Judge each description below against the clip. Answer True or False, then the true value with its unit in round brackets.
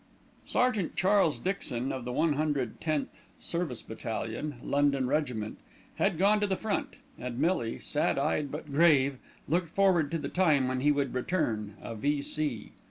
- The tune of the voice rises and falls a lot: False (4.8 semitones)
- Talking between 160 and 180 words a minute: False (150 wpm)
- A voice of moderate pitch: True (145 Hz)